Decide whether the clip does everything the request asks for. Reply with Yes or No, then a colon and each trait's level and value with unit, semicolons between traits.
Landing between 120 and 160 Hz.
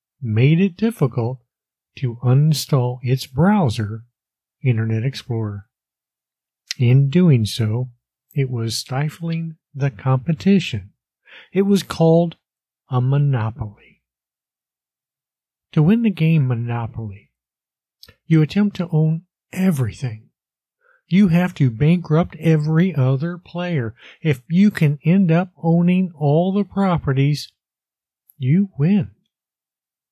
Yes: low, 135 Hz